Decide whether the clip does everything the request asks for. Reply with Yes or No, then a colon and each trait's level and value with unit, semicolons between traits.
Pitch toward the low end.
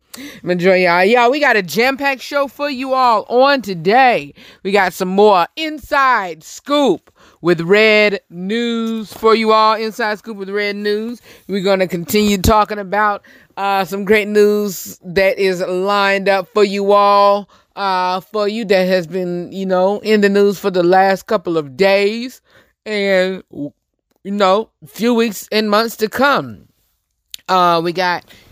No: high, 200 Hz